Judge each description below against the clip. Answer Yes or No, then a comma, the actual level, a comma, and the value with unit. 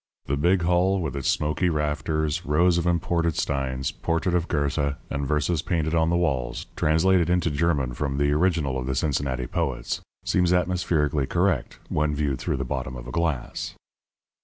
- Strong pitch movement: No, average, 3.6 semitones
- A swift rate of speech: No, average, 170 wpm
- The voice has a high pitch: No, very low, 75 Hz